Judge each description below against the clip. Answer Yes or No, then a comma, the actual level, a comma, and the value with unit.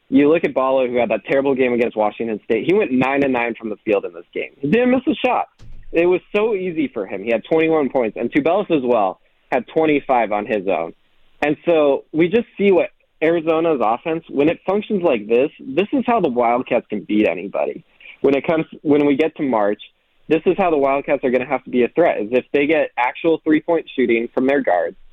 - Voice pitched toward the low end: No, medium, 145 Hz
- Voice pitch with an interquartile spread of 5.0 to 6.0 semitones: Yes, wide, 5.5 semitones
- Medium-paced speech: No, fast, 235 wpm